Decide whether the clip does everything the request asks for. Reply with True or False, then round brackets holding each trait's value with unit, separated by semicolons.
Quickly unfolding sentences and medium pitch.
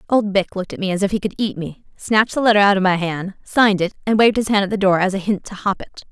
False (325 wpm; 200 Hz)